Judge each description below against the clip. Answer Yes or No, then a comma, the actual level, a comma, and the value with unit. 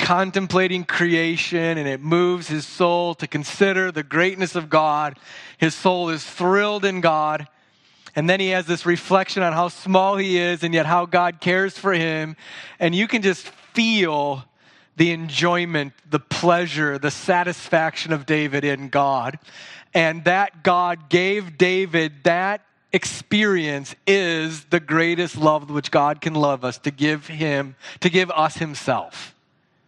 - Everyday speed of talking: Yes, average, 150 wpm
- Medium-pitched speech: Yes, medium, 170 Hz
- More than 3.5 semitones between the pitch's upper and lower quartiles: No, average, 3.1 semitones